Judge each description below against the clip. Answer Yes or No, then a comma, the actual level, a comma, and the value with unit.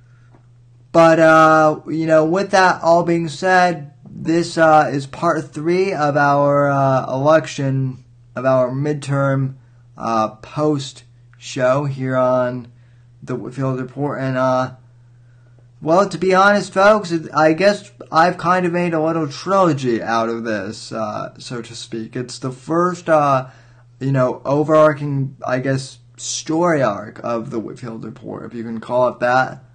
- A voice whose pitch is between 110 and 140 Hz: Yes, low, 135 Hz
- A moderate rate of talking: Yes, average, 150 wpm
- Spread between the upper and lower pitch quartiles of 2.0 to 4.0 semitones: No, average, 4.7 semitones